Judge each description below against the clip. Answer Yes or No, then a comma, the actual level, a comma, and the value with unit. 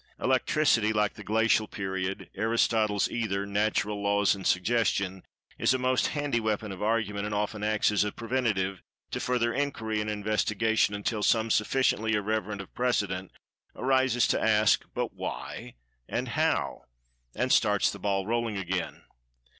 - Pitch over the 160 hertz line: No, low, 105 Hz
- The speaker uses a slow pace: No, average, 145 wpm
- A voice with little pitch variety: Yes, narrow, 2.2 semitones